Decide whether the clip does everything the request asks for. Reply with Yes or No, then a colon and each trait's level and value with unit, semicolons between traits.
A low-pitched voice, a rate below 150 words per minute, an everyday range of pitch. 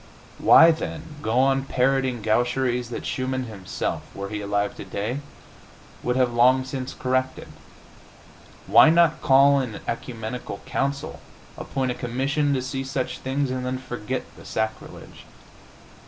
No: low, 130 Hz; average, 140 wpm; narrow, 2.1 semitones